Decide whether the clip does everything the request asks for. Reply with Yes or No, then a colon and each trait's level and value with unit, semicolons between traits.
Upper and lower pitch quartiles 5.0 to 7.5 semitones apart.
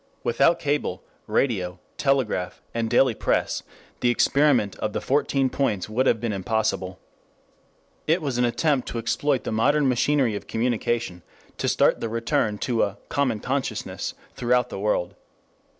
No: average, 4.1 semitones